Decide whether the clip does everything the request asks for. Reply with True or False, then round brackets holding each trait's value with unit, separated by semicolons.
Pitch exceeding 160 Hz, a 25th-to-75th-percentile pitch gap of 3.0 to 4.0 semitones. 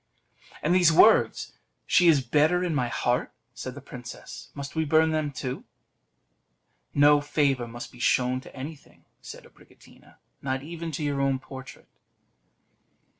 False (140 Hz; 3.5 semitones)